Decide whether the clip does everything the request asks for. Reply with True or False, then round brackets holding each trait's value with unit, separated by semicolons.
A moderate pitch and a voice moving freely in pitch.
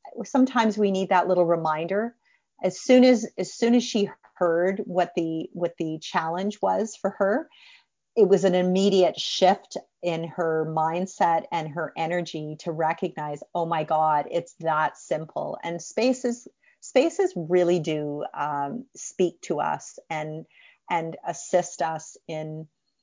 False (175 Hz; 4.1 semitones)